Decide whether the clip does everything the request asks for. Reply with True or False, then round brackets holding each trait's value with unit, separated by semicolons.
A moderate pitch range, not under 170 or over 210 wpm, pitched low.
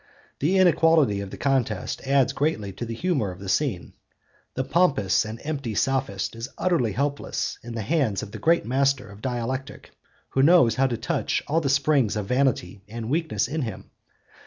True (5.0 semitones; 180 wpm; 130 Hz)